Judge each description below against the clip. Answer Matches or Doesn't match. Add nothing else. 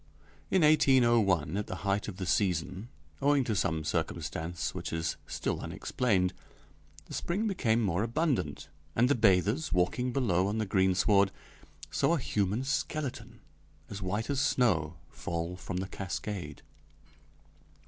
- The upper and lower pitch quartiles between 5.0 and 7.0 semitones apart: Matches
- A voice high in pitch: Doesn't match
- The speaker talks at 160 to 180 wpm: Doesn't match